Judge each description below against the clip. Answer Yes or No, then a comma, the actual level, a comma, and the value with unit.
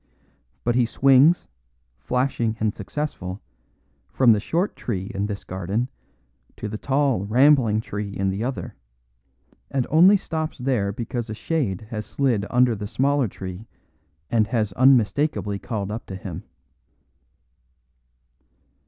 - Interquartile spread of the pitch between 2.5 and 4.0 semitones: No, average, 4.7 semitones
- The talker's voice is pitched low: Yes, low, 115 Hz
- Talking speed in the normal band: No, slow, 130 wpm